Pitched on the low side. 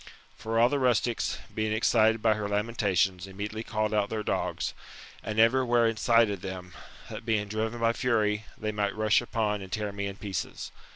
Yes: low, 110 Hz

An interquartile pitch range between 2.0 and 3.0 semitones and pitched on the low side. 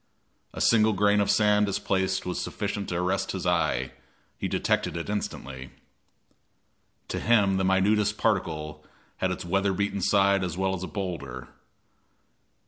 Yes: average, 2.7 semitones; very low, 95 Hz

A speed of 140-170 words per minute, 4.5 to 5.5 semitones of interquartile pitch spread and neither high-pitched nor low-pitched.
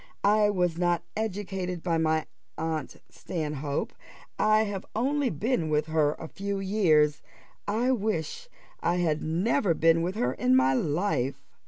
Yes: average, 145 wpm; average, 4.8 semitones; medium, 175 Hz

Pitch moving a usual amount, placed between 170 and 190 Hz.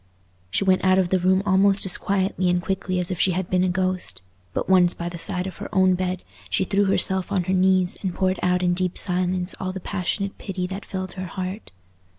No: narrow, 0.9 semitones; medium, 185 Hz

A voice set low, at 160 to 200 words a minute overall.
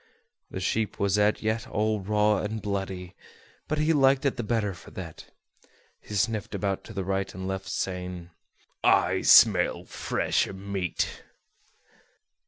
No: low, 100 Hz; average, 145 wpm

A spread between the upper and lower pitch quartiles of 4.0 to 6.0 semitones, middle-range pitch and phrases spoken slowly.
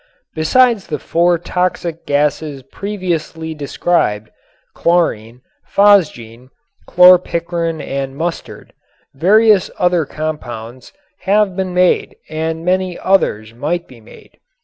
Yes: average, 4.6 semitones; medium, 165 Hz; slow, 95 wpm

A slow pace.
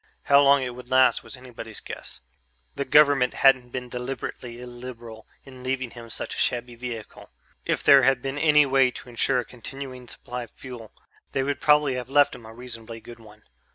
No: average, 190 wpm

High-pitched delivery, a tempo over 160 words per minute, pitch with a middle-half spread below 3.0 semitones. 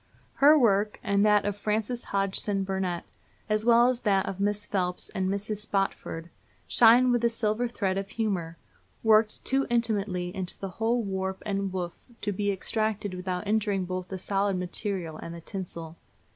Yes: high, 200 Hz; average, 170 wpm; narrow, 2.6 semitones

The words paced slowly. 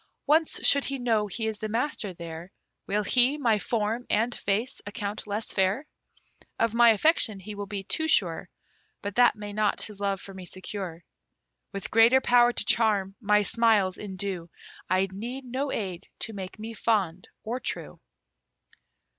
No: average, 165 wpm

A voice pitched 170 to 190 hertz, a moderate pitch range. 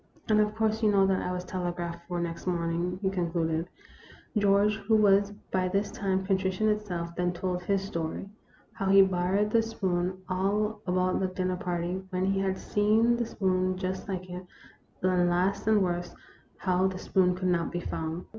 No: medium, 185 Hz; narrow, 1.9 semitones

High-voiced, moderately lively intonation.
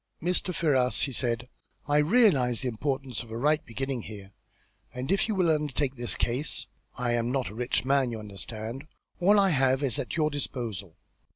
No: low, 130 Hz; average, 4.0 semitones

